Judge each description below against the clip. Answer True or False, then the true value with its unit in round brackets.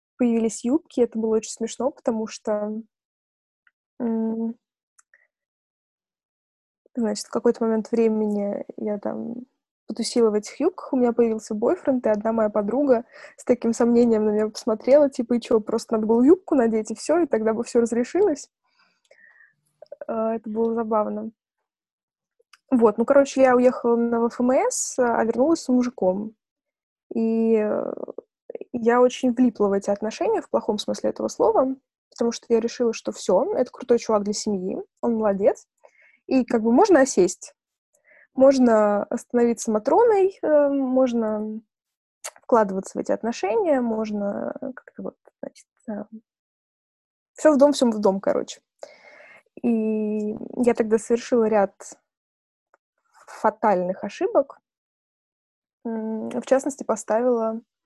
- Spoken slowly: False (125 wpm)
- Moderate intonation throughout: True (3.5 semitones)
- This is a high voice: True (235 Hz)